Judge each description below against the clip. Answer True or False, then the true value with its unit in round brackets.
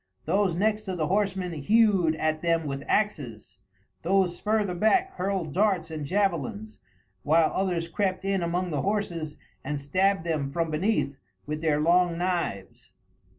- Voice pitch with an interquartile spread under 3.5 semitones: False (3.9 semitones)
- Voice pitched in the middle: True (175 Hz)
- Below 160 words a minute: True (150 wpm)